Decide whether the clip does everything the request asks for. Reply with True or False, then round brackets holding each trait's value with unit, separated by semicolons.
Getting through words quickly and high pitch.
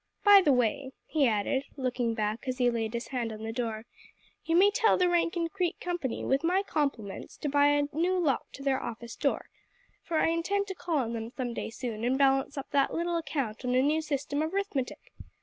True (220 wpm; 275 Hz)